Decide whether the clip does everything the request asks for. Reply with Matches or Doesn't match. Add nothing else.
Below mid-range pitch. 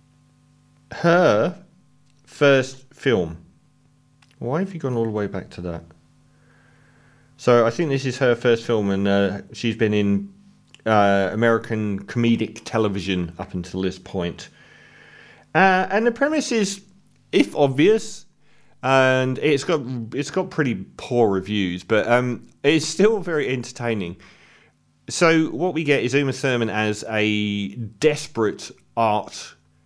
Matches